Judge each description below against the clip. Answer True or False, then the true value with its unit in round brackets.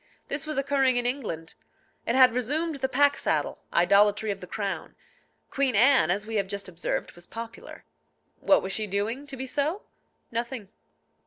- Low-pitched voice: False (235 Hz)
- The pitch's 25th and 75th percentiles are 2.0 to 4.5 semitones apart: False (5.4 semitones)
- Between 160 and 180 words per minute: True (170 wpm)